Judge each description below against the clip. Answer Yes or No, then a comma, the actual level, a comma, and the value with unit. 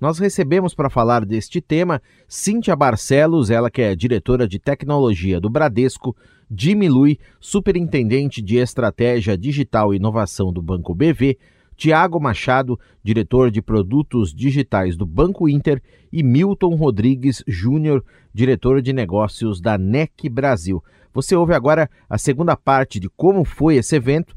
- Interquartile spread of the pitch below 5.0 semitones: No, wide, 5.4 semitones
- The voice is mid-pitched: No, low, 130 Hz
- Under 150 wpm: Yes, average, 140 wpm